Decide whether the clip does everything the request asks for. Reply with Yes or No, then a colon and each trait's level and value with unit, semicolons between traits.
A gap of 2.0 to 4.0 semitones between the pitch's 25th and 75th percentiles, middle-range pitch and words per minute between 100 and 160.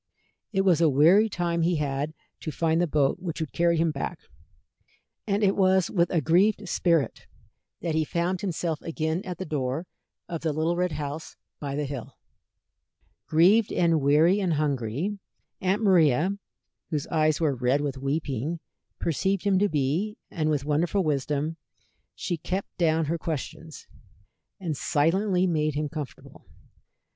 Yes: average, 3.2 semitones; medium, 160 Hz; average, 155 wpm